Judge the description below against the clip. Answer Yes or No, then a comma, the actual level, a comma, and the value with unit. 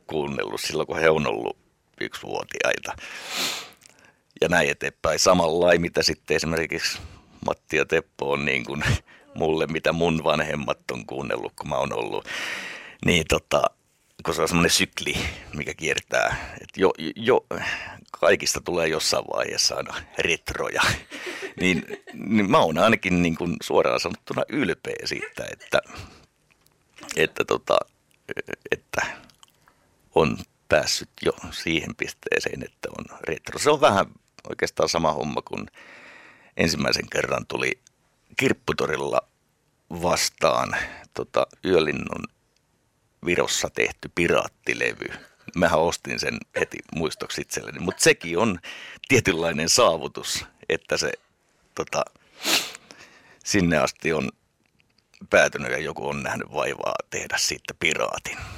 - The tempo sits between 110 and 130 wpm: Yes, average, 120 wpm